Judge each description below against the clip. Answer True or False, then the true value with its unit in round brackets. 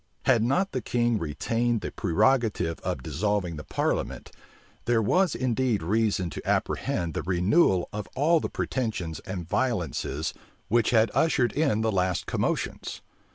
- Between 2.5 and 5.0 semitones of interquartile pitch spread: False (5.6 semitones)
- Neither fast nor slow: True (150 wpm)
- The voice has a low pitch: True (110 Hz)